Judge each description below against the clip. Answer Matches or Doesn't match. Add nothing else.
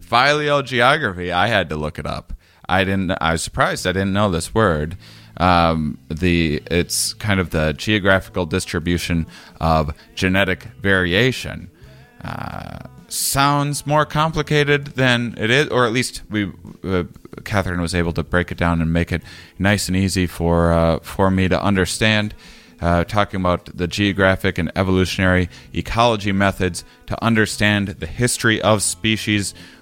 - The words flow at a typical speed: Matches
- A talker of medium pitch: Doesn't match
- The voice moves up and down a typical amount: Matches